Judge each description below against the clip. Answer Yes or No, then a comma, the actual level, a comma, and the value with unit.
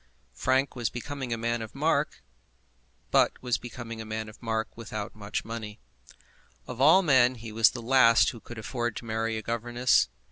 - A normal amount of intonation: No, narrow, 1.9 semitones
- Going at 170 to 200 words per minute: Yes, average, 180 wpm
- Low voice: Yes, low, 115 Hz